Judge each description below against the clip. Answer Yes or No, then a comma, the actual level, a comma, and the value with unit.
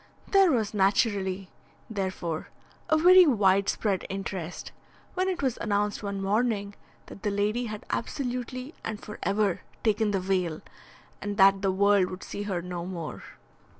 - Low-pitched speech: No, high, 205 Hz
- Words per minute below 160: Yes, average, 150 wpm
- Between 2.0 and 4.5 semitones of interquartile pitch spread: Yes, average, 2.9 semitones